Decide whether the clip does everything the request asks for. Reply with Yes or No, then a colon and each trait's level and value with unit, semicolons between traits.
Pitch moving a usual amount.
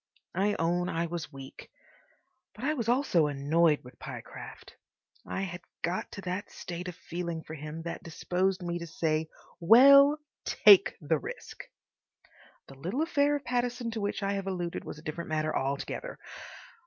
Yes: average, 4.6 semitones